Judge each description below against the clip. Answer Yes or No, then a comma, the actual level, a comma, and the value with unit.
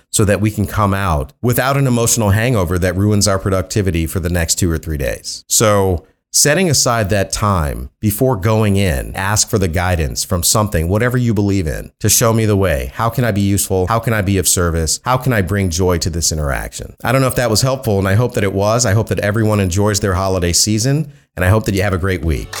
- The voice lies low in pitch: Yes, low, 100 Hz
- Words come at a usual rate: No, fast, 245 wpm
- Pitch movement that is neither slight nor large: Yes, average, 3.6 semitones